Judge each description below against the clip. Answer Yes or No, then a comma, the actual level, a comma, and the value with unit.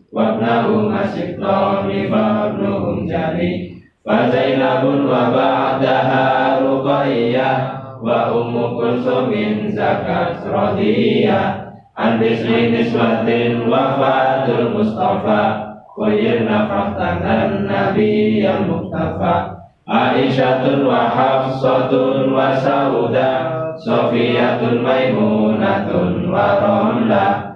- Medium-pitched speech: No, low, 130 Hz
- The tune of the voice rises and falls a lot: No, average, 2.7 semitones